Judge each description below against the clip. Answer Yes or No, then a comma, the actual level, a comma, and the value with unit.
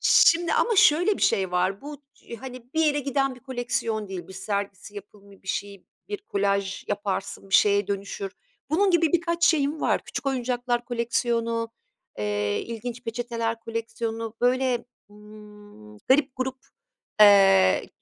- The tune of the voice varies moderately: Yes, average, 4.7 semitones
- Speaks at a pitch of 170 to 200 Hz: No, high, 230 Hz